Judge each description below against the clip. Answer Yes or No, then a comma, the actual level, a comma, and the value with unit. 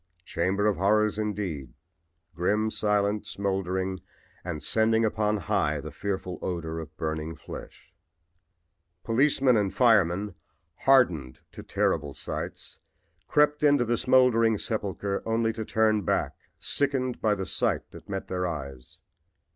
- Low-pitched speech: Yes, low, 105 Hz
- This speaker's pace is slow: Yes, slow, 125 wpm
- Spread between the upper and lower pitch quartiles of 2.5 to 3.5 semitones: No, average, 3.9 semitones